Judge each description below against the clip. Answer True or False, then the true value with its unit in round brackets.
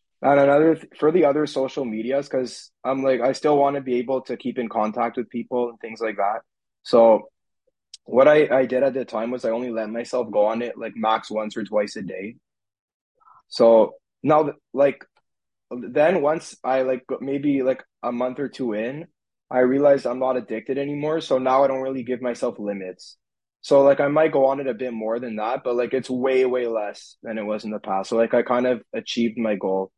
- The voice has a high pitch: False (125 Hz)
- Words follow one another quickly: True (220 wpm)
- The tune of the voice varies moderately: True (3.1 semitones)